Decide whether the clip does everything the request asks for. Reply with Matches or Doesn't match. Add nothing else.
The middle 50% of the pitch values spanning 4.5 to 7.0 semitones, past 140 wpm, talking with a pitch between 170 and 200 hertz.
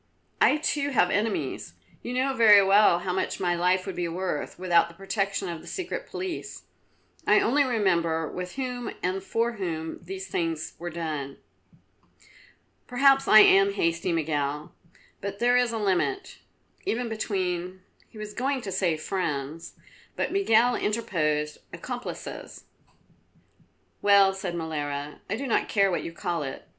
Matches